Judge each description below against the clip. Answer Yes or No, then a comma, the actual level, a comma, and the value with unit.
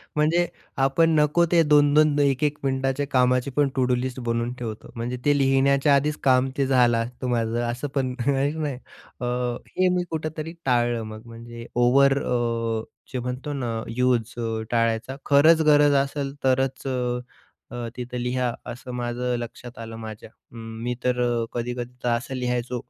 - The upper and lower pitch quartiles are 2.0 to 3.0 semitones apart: Yes, average, 2.7 semitones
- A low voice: Yes, low, 125 Hz